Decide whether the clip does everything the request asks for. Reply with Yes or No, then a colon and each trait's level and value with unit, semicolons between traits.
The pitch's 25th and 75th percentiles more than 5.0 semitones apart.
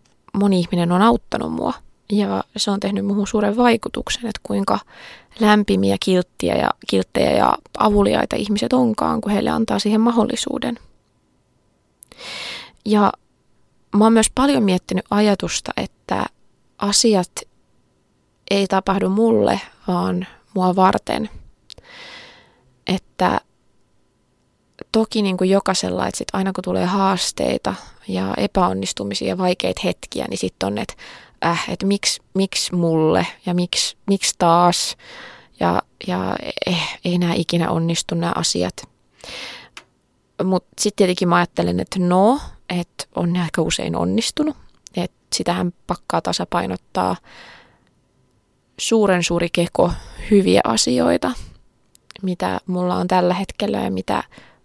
No: average, 3.4 semitones